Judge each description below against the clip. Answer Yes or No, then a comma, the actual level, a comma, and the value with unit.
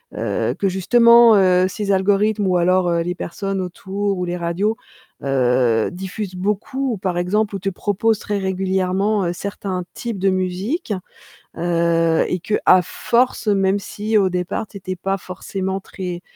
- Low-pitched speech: No, high, 190 Hz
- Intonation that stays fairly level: Yes, narrow, 2.2 semitones